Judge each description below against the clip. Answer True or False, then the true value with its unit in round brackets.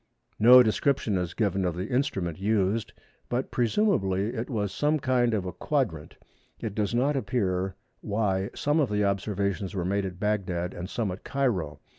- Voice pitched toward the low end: True (105 Hz)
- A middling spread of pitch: True (4.5 semitones)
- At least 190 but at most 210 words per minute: False (170 wpm)